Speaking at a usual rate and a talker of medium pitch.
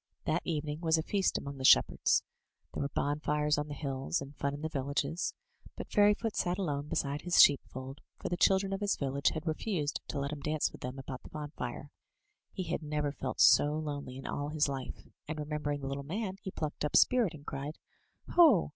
No: fast, 215 wpm; medium, 150 Hz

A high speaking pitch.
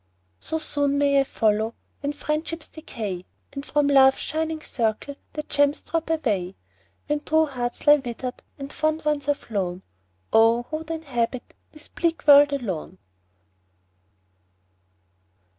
Yes: very high, 285 Hz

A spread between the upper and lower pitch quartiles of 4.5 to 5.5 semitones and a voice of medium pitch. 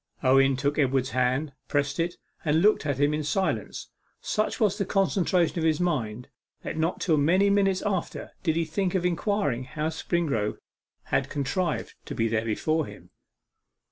Yes: average, 5.0 semitones; medium, 155 Hz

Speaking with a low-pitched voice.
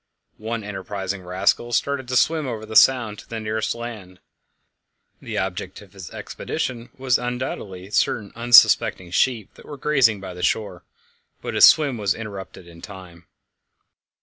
Yes: low, 105 Hz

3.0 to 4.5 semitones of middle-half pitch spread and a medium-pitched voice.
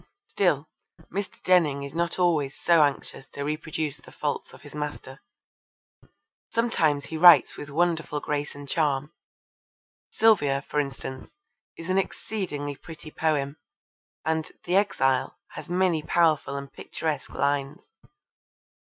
Yes: average, 3.3 semitones; medium, 150 Hz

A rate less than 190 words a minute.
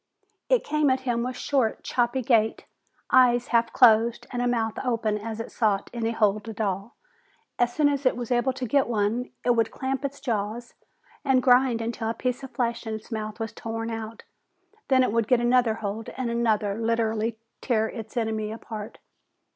No: average, 195 wpm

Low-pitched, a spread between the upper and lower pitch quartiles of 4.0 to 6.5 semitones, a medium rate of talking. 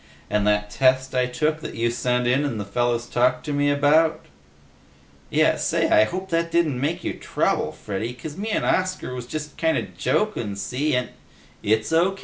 Yes: low, 130 Hz; average, 4.9 semitones; average, 190 wpm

